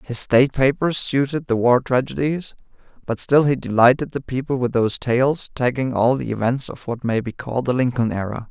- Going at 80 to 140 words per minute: No, average, 200 wpm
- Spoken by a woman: No, male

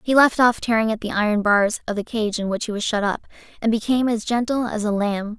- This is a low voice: No, high, 220 Hz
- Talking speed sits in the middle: No, fast, 265 wpm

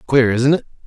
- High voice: No, low, 130 Hz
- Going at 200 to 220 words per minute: Yes, fast, 210 wpm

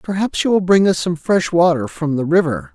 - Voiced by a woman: No, male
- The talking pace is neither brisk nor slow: No, fast, 240 wpm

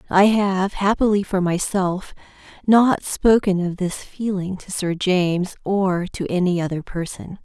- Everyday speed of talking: Yes, average, 145 wpm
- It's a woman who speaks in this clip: Yes, female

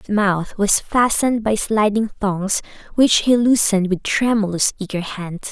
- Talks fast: No, average, 150 wpm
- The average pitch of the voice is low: No, high, 210 Hz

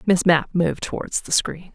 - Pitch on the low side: No, medium, 170 Hz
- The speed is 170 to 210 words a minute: Yes, fast, 205 wpm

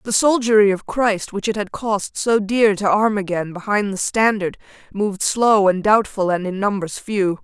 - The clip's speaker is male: No, female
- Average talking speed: Yes, average, 195 wpm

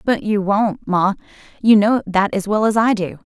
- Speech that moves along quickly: Yes, fast, 215 wpm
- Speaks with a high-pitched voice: Yes, high, 205 Hz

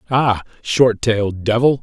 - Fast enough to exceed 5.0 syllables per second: No, 4.2 syllables/s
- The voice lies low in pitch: Yes, low, 115 Hz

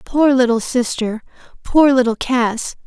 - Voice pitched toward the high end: Yes, very high, 250 Hz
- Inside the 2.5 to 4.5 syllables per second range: Yes, 4.0 syllables/s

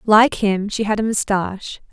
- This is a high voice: Yes, high, 210 Hz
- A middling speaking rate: Yes, average, 190 wpm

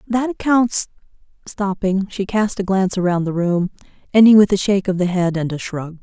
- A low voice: No, high, 195 Hz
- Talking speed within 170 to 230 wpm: Yes, average, 200 wpm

